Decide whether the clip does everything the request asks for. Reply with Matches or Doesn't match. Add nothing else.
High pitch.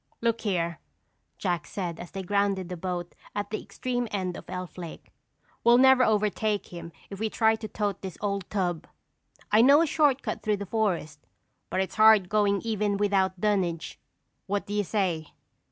Matches